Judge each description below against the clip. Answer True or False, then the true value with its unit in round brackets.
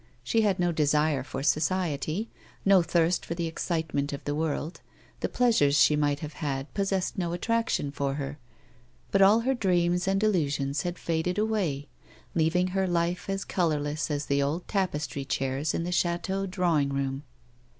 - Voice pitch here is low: False (165 Hz)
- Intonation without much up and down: False (4.3 semitones)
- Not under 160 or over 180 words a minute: True (165 wpm)